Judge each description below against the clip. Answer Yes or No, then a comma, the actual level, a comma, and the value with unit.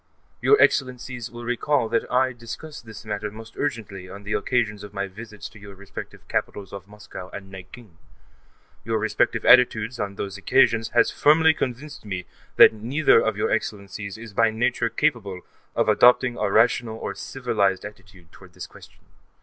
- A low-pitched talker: Yes, low, 110 Hz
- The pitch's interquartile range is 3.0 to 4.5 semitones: Yes, average, 3.4 semitones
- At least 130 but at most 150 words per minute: No, average, 170 wpm